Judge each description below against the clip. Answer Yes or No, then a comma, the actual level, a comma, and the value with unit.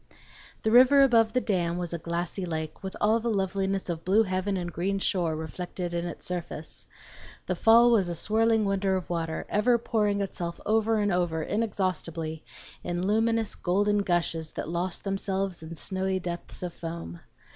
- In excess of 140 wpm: Yes, average, 170 wpm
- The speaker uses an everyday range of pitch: Yes, average, 3.4 semitones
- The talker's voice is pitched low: No, high, 190 Hz